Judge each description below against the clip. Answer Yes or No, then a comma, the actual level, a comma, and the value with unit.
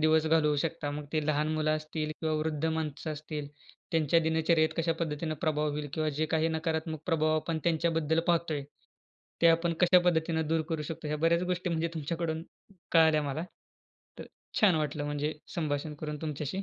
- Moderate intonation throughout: No, narrow, 1.3 semitones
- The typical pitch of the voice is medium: Yes, medium, 160 Hz